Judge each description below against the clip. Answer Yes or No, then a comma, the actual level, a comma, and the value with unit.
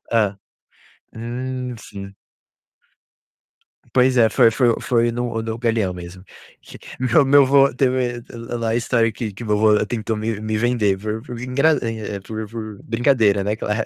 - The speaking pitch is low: Yes, low, 115 Hz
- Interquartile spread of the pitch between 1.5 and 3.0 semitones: Yes, narrow, 2.5 semitones